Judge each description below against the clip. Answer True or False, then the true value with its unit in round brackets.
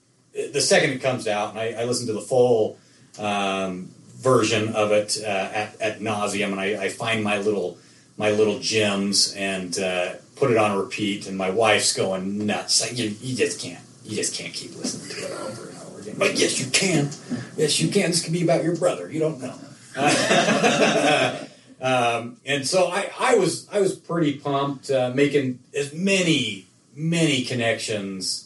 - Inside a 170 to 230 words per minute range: True (190 wpm)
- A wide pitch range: True (5.7 semitones)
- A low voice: True (115 Hz)